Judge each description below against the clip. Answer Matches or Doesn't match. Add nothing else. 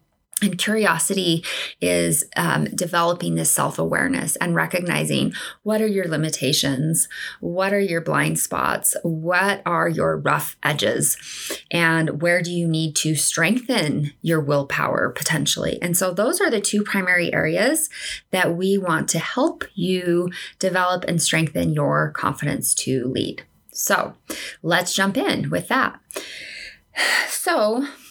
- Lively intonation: Doesn't match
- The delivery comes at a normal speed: Doesn't match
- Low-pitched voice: Doesn't match